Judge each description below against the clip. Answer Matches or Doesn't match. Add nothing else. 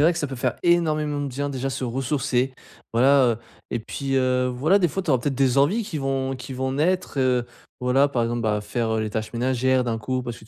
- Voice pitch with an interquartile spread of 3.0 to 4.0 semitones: Doesn't match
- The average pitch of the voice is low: Matches